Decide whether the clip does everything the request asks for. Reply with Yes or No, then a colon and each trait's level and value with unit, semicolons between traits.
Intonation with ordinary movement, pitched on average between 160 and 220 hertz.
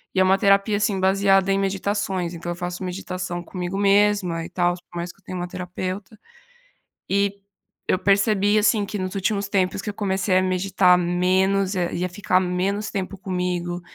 No: narrow, 1.7 semitones; high, 190 Hz